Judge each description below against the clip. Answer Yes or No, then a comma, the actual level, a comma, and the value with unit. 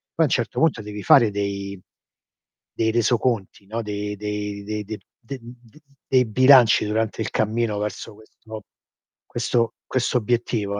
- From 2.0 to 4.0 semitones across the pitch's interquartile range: Yes, narrow, 2.4 semitones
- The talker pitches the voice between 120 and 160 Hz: No, low, 110 Hz